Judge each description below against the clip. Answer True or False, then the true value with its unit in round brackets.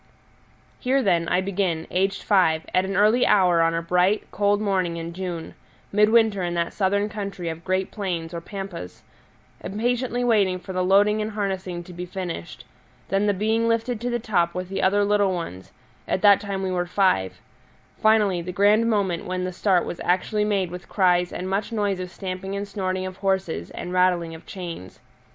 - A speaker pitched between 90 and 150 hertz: False (190 Hz)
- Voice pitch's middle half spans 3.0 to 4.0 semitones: False (2.5 semitones)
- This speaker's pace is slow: False (190 wpm)